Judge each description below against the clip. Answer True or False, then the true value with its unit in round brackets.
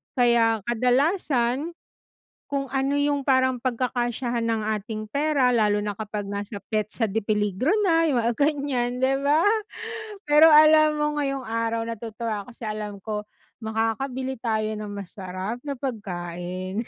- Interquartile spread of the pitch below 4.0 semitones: False (4.3 semitones)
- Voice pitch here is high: True (235 Hz)